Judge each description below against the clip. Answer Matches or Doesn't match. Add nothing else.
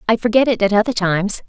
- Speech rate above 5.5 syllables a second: Matches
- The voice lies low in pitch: Doesn't match